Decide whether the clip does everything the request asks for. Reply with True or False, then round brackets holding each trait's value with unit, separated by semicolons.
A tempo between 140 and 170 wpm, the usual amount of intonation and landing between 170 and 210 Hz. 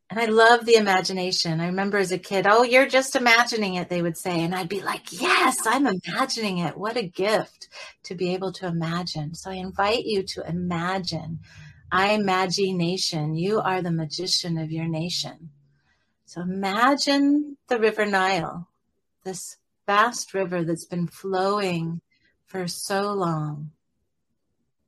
True (150 wpm; 3.3 semitones; 185 Hz)